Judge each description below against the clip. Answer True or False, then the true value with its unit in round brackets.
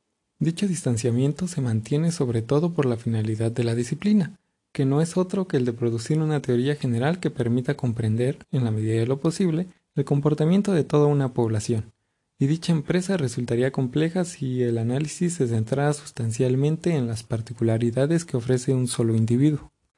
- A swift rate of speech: False (170 wpm)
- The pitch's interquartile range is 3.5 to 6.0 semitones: True (4.8 semitones)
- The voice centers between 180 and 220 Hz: False (135 Hz)